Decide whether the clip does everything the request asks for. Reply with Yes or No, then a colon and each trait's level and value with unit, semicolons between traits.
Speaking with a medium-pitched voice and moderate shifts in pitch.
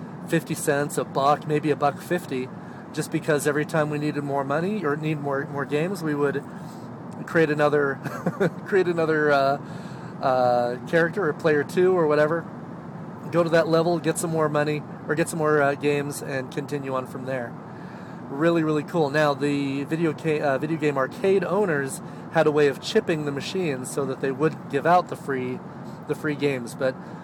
Yes: medium, 150 Hz; average, 3.0 semitones